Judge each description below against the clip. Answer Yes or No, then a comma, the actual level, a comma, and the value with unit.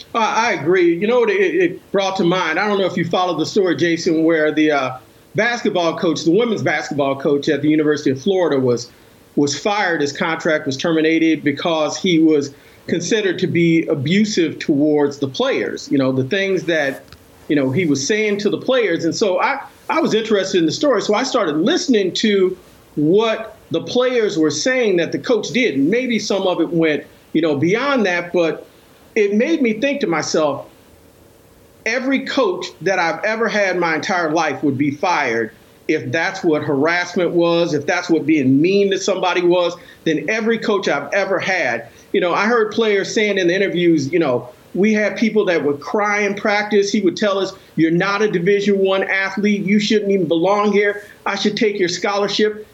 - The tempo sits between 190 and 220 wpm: Yes, average, 195 wpm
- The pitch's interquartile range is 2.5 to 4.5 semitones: No, average, 5.1 semitones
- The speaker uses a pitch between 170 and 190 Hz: Yes, medium, 185 Hz